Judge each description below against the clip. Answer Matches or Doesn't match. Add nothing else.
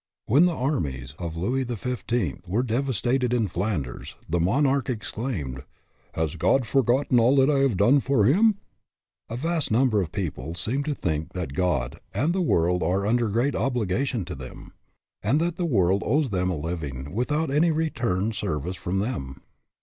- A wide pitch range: Matches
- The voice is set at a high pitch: Doesn't match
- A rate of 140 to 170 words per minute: Doesn't match